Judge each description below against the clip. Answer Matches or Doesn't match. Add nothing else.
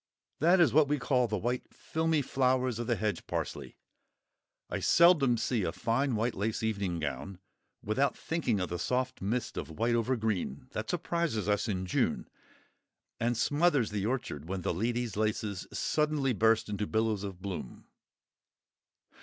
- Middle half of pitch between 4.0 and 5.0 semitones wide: Matches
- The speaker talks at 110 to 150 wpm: Doesn't match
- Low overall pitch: Matches